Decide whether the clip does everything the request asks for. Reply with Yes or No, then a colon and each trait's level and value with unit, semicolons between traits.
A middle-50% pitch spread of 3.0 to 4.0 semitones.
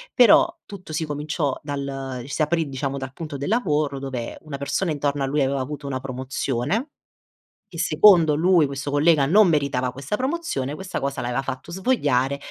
Yes: average, 3.6 semitones